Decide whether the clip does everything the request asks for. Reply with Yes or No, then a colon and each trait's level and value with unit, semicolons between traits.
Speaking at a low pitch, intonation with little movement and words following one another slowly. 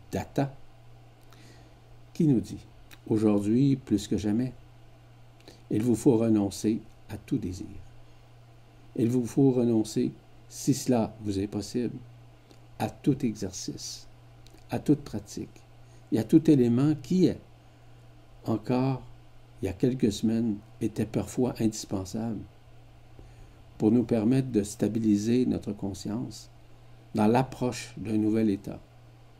Yes: low, 115 Hz; narrow, 1.9 semitones; slow, 115 wpm